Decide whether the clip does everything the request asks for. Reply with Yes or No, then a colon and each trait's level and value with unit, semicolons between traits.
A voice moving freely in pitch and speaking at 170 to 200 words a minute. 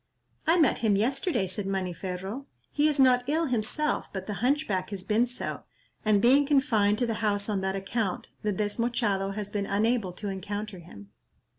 No: average, 4.1 semitones; average, 175 wpm